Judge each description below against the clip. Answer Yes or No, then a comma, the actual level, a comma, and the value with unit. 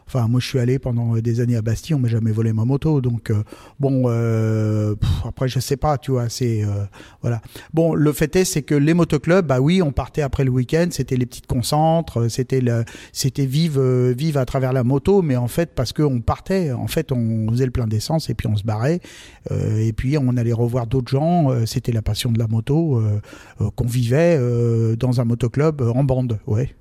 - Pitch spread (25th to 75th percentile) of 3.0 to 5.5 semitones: Yes, average, 3.5 semitones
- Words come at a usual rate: No, fast, 230 wpm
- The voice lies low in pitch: Yes, low, 125 Hz